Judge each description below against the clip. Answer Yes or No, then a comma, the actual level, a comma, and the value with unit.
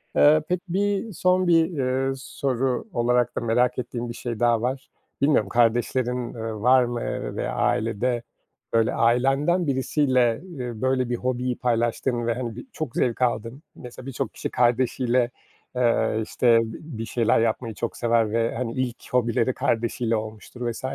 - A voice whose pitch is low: Yes, low, 125 Hz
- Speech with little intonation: Yes, narrow, 2.0 semitones